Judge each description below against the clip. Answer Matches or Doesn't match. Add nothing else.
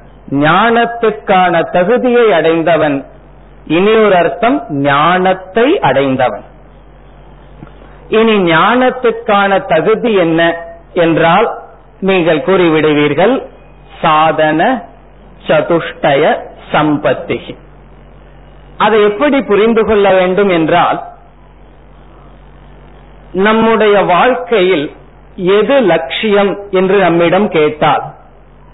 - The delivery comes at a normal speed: Doesn't match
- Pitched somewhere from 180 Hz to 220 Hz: Matches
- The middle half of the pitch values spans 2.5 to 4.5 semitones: Doesn't match